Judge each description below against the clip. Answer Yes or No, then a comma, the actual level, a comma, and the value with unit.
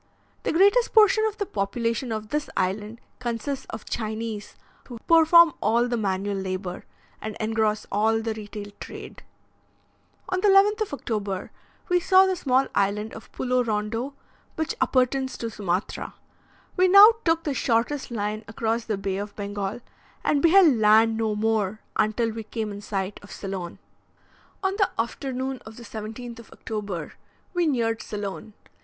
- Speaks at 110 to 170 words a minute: Yes, average, 155 wpm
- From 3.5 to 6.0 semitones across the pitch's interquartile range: Yes, average, 4.6 semitones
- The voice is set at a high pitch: Yes, high, 225 Hz